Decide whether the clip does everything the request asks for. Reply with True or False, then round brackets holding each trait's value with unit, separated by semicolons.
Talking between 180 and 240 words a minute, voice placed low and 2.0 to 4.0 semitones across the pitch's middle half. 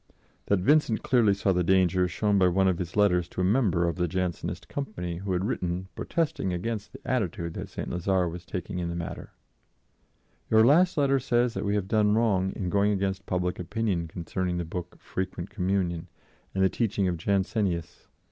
True (195 wpm; 95 Hz; 3.0 semitones)